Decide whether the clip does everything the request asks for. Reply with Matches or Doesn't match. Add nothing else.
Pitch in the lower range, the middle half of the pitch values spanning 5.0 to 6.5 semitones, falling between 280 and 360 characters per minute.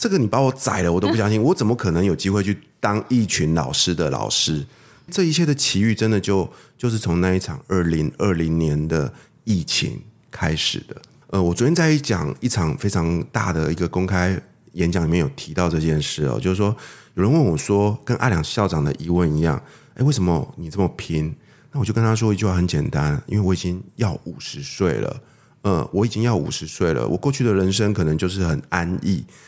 Matches